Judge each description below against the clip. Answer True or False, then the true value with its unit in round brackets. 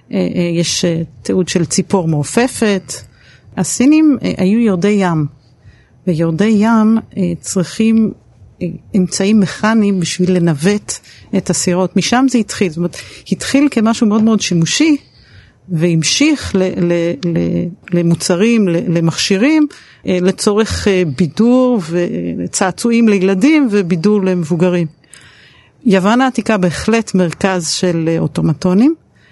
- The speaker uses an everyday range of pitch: True (4.5 semitones)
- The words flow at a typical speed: False (95 wpm)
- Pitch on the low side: False (185 Hz)